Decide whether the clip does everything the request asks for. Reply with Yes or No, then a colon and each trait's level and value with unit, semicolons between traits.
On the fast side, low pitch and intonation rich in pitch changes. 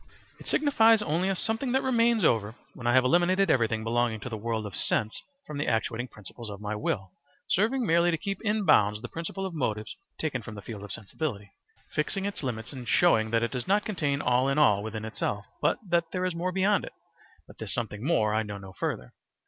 Yes: fast, 220 wpm; low, 125 Hz; wide, 9.0 semitones